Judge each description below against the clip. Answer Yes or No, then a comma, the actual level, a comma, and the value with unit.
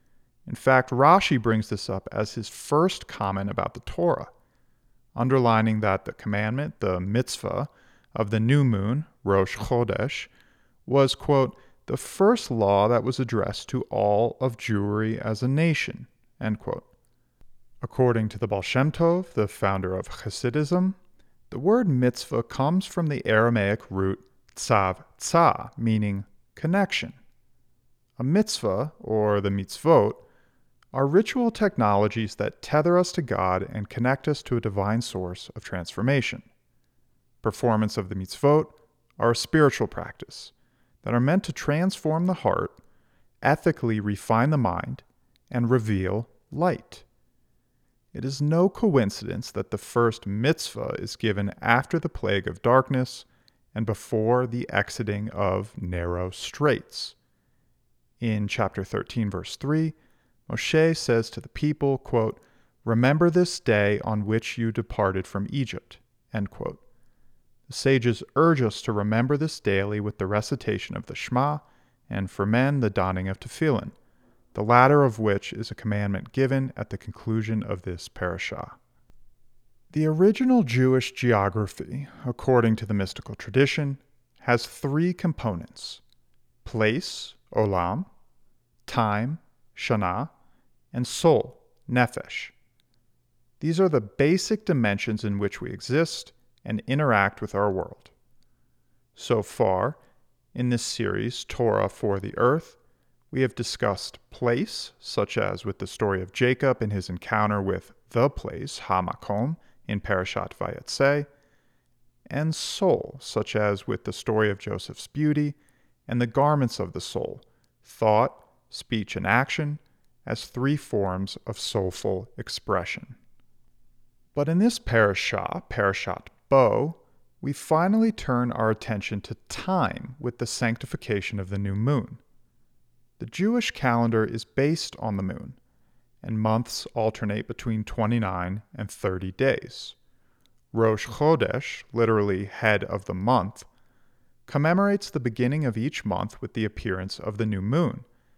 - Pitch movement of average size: Yes, average, 4.8 semitones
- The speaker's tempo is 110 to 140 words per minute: Yes, slow, 135 wpm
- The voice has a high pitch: No, low, 115 Hz